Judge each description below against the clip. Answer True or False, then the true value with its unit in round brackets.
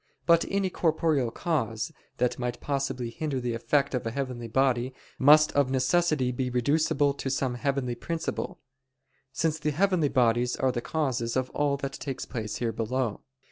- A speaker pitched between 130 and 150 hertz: True (135 Hz)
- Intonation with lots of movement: False (3.5 semitones)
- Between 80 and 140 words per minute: False (165 wpm)